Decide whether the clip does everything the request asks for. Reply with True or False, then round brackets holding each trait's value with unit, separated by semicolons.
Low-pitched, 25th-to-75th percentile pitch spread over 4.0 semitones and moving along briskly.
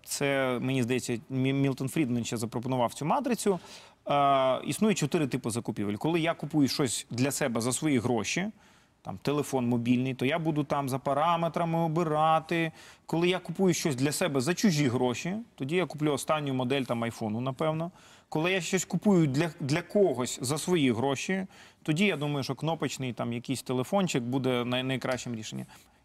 False (145 Hz; 4.9 semitones; 165 wpm)